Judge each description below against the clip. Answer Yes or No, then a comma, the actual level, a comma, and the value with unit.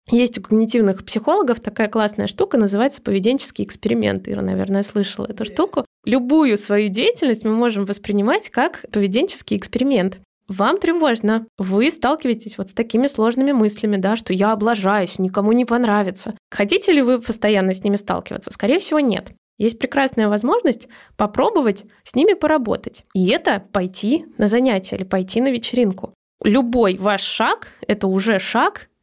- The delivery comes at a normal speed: Yes, average, 150 wpm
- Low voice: No, high, 220 Hz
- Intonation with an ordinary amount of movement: Yes, average, 3.9 semitones